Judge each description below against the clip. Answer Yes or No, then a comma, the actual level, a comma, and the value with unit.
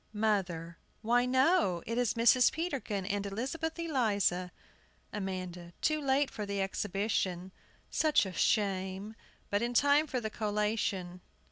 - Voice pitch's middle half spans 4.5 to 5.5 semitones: Yes, average, 5.1 semitones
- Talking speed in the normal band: No, slow, 130 wpm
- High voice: Yes, high, 210 Hz